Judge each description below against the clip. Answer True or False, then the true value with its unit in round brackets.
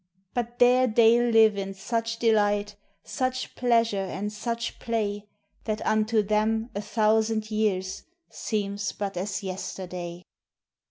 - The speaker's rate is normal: False (120 wpm)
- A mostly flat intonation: True (2.2 semitones)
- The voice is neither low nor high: False (215 Hz)